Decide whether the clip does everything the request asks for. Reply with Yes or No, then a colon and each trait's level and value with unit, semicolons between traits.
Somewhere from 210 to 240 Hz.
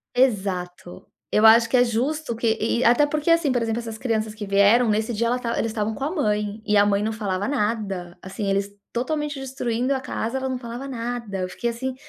Yes: high, 230 Hz